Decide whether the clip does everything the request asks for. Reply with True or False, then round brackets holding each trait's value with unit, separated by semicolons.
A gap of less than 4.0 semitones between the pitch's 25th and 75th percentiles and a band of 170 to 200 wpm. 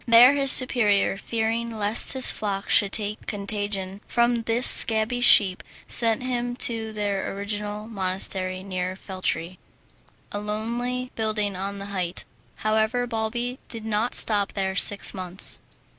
False (2.7 semitones; 135 wpm)